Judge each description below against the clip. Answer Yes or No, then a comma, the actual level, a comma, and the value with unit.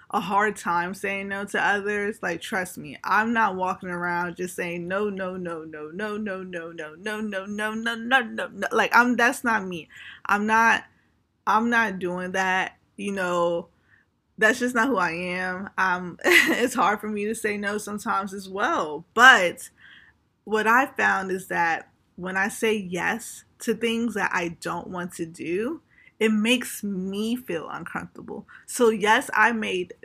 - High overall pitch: Yes, high, 200 Hz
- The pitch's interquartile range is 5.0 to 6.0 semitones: No, average, 3.3 semitones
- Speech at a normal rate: Yes, average, 175 wpm